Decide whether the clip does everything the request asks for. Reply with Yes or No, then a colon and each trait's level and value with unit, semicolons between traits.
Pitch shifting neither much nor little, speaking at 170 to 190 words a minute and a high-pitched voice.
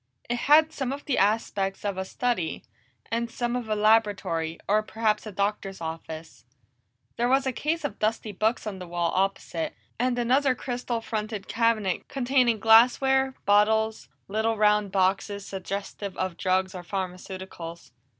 No: average, 4.0 semitones; average, 150 wpm; high, 215 Hz